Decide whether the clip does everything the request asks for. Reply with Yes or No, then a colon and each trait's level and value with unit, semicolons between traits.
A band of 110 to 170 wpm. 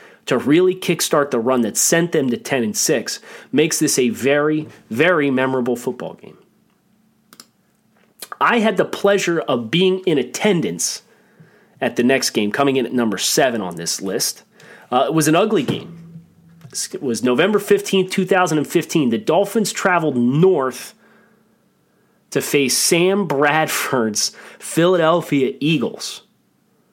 Yes: average, 145 wpm